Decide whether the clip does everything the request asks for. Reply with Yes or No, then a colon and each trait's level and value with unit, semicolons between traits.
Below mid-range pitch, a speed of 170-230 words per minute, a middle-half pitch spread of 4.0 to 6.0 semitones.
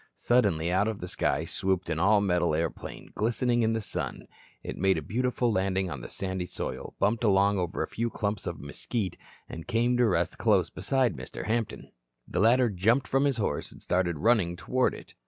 Yes: low, 100 Hz; average, 195 wpm; average, 4.7 semitones